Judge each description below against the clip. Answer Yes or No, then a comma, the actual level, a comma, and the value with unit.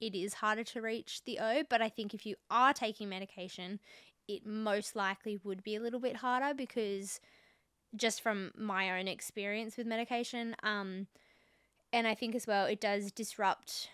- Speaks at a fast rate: No, average, 175 wpm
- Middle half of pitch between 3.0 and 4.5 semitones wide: No, narrow, 2.5 semitones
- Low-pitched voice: No, high, 215 Hz